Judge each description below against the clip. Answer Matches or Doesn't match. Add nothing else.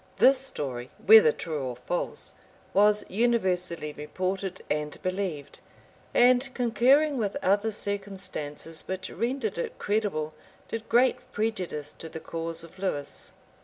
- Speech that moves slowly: Matches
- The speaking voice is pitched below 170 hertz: Doesn't match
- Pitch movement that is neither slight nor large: Doesn't match